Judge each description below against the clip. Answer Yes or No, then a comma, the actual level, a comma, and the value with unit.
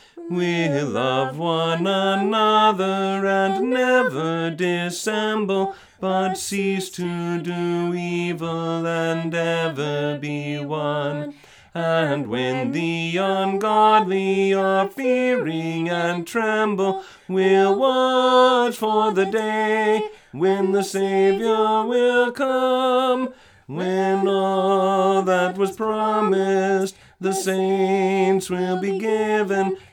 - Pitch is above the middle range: Yes, high, 195 Hz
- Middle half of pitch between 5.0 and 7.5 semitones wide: No, average, 4.0 semitones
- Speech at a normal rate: No, slow, 90 wpm